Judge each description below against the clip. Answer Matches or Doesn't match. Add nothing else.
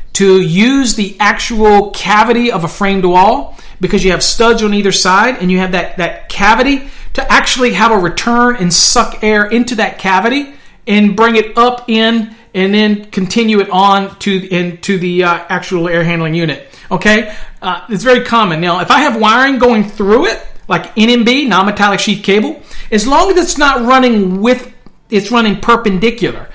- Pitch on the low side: Doesn't match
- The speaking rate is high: Doesn't match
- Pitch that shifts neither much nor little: Matches